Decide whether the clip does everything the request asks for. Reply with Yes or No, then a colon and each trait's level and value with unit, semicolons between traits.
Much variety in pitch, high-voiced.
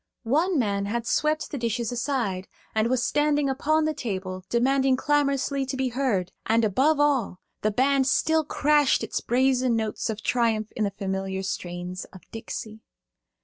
No: average, 4.9 semitones; high, 245 Hz